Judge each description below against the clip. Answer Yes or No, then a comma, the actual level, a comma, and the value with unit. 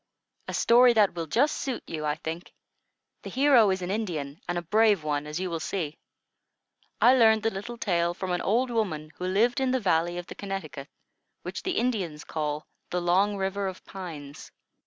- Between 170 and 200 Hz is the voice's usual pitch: Yes, high, 190 Hz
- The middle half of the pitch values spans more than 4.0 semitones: Yes, wide, 5.5 semitones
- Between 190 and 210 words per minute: Yes, average, 195 wpm